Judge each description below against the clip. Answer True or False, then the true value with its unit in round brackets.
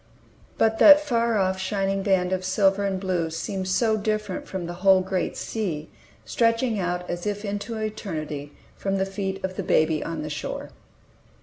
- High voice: True (195 Hz)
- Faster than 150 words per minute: True (175 wpm)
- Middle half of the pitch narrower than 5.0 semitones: True (2.9 semitones)